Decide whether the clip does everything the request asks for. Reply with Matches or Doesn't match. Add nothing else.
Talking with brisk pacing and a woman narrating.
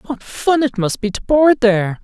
Doesn't match